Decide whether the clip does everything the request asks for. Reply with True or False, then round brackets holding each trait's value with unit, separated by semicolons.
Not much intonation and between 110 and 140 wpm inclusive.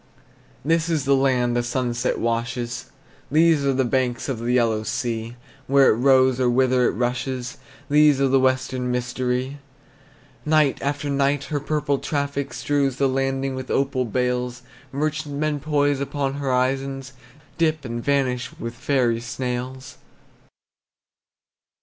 True (2.3 semitones; 135 wpm)